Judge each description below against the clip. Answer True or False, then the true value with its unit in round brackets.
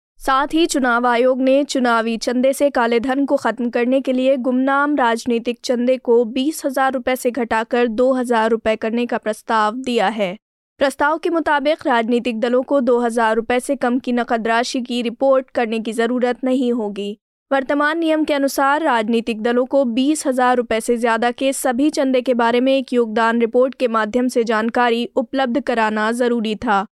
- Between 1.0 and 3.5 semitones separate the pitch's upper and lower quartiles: True (2.5 semitones)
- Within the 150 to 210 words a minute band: True (180 wpm)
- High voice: True (250 Hz)